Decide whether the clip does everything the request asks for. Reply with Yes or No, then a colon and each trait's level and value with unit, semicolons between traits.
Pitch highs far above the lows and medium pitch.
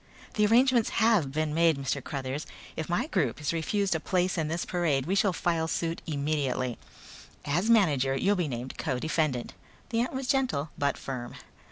Yes: wide, 5.7 semitones; medium, 160 Hz